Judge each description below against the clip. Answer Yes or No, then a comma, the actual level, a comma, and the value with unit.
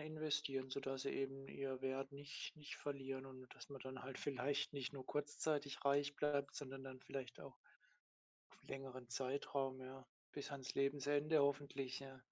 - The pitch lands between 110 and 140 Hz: Yes, low, 135 Hz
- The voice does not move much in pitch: Yes, narrow, 1.4 semitones